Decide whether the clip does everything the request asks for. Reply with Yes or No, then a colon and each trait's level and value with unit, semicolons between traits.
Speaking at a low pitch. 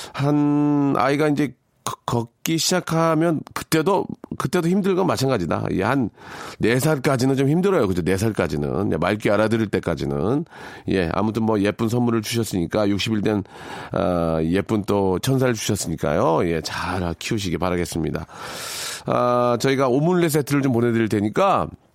Yes: low, 115 Hz